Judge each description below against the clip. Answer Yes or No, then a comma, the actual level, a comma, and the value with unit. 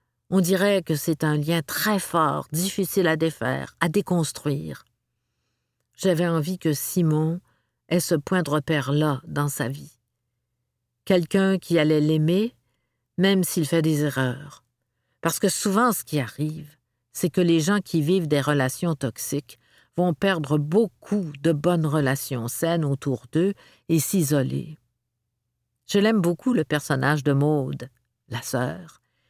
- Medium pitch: Yes, medium, 155 Hz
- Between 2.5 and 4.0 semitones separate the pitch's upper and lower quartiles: No, average, 4.5 semitones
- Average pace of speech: No, slow, 140 wpm